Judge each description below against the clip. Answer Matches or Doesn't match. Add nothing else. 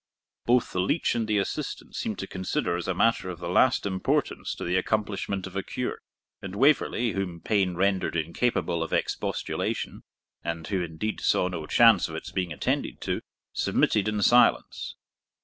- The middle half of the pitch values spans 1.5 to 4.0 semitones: Matches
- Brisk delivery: Doesn't match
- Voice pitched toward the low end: Matches